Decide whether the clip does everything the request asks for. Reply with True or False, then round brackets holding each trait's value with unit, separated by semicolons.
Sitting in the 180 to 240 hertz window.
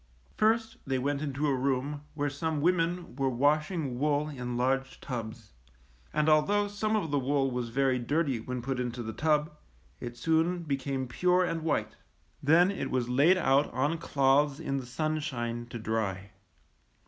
False (140 Hz)